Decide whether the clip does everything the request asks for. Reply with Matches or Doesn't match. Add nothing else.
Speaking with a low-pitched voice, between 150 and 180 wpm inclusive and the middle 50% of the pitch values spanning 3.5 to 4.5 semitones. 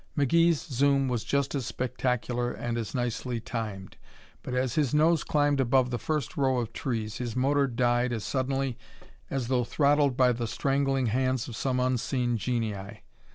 Doesn't match